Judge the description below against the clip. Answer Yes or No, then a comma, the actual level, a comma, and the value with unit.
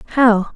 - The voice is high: Yes, high, 225 Hz